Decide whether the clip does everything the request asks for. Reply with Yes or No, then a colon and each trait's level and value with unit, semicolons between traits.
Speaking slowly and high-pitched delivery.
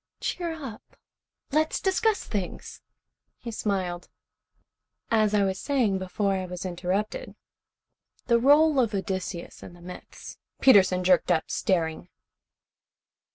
Yes: slow, 120 wpm; high, 200 Hz